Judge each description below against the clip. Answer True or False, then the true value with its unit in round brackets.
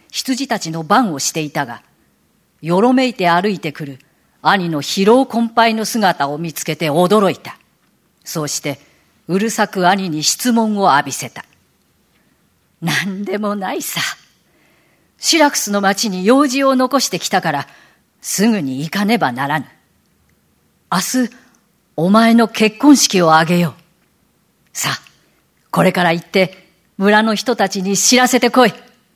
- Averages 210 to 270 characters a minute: True (250 characters per minute)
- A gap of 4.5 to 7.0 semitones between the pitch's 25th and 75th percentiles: True (5.3 semitones)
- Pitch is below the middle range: False (195 Hz)